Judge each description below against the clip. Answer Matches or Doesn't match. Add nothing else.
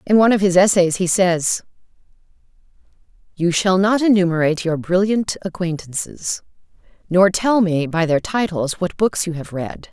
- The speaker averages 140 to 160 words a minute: Matches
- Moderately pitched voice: Matches